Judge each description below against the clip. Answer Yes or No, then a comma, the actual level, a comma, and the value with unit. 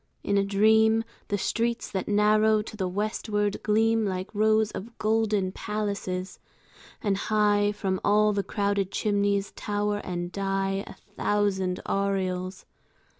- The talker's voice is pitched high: Yes, high, 205 Hz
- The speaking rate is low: Yes, slow, 130 wpm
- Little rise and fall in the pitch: Yes, narrow, 1.6 semitones